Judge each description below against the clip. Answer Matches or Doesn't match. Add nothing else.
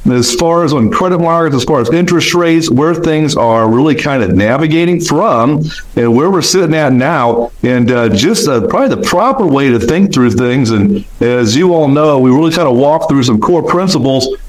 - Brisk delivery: Matches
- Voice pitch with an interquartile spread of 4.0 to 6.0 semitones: Matches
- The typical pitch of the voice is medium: Matches